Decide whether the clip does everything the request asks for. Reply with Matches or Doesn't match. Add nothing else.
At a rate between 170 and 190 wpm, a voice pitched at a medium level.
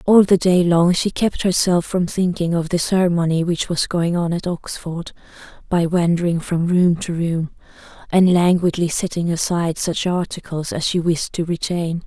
Matches